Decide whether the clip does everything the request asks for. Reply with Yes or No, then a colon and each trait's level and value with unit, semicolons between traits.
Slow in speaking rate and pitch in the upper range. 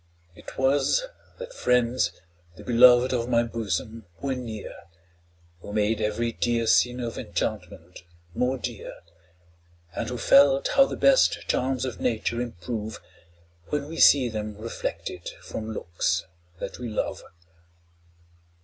No: slow, 125 wpm; low, 120 Hz